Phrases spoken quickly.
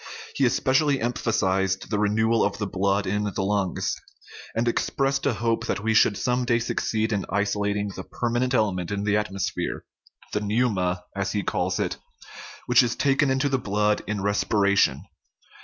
No: average, 165 wpm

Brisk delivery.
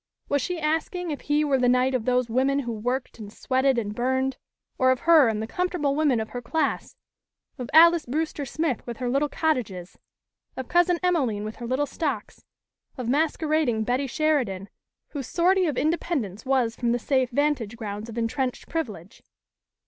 No: average, 180 wpm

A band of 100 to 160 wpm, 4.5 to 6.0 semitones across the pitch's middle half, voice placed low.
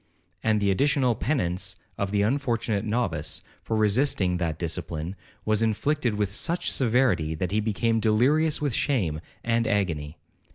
Yes: average, 140 wpm; average, 5.1 semitones; low, 105 Hz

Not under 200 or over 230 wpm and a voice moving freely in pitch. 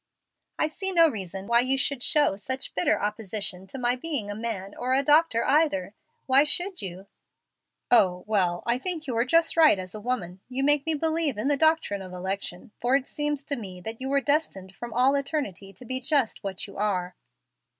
Yes: fast, 205 wpm; wide, 6.7 semitones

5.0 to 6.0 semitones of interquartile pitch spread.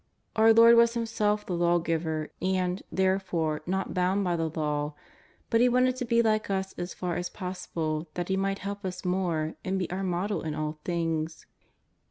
No: average, 3.5 semitones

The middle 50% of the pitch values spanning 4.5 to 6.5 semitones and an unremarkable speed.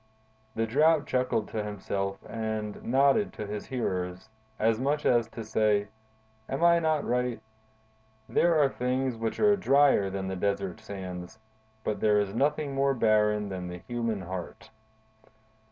Yes: average, 4.8 semitones; average, 155 wpm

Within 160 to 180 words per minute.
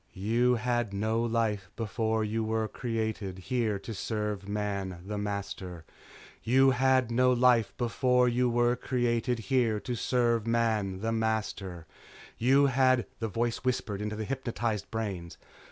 No: average, 150 wpm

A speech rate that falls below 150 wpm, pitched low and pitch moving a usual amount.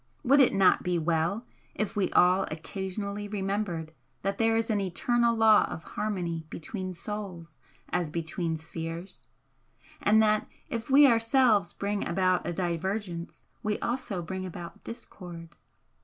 No: average, 140 wpm; high, 190 Hz; average, 3.9 semitones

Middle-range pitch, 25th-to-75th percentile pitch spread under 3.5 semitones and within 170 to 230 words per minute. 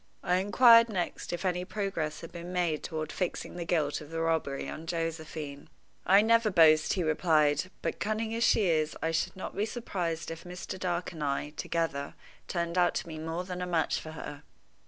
Yes: medium, 170 Hz; average, 2.7 semitones; average, 200 wpm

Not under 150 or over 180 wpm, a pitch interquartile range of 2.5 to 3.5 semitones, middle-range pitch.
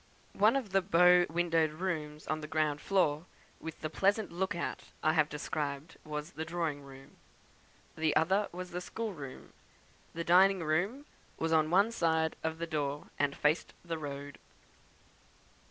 Yes: average, 155 wpm; average, 3.0 semitones; medium, 160 Hz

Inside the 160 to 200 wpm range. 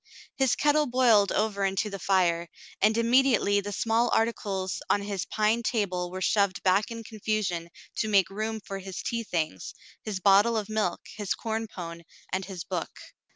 Yes: average, 170 wpm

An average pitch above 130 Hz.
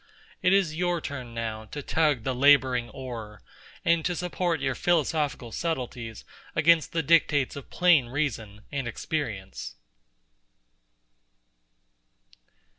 Yes: medium, 140 Hz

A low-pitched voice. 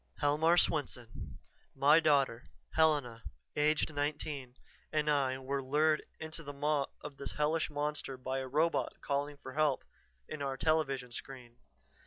No: medium, 145 Hz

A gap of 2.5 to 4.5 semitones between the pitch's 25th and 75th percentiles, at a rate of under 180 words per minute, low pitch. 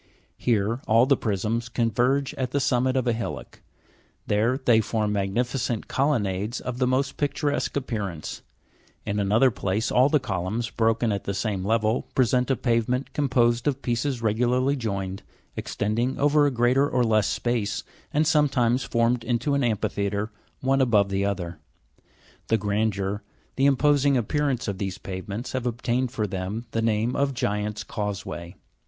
Yes: average, 3.8 semitones; average, 160 wpm; low, 115 Hz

